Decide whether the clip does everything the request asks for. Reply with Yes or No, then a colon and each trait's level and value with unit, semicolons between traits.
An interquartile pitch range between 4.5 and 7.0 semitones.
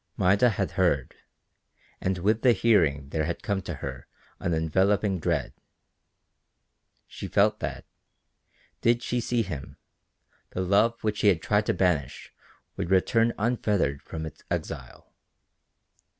Yes: average, 5.1 semitones